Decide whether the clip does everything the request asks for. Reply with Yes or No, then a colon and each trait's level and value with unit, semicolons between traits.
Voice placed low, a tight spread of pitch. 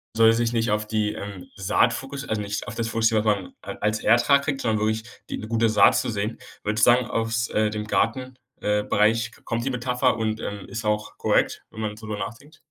Yes: low, 110 Hz; narrow, 1.7 semitones